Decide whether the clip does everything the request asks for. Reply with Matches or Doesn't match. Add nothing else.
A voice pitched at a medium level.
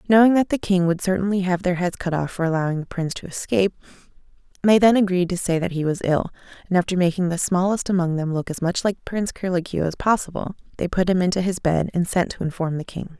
Matches